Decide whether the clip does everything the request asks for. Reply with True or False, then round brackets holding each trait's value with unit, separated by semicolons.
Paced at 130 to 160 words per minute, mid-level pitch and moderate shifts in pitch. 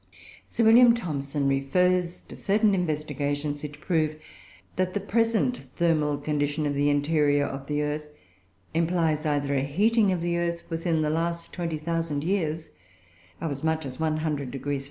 True (155 wpm; 155 Hz; 3.0 semitones)